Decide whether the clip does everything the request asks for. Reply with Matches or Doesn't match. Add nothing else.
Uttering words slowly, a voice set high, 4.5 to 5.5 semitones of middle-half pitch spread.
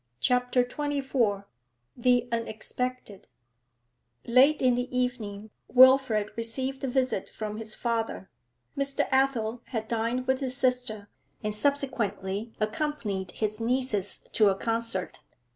Doesn't match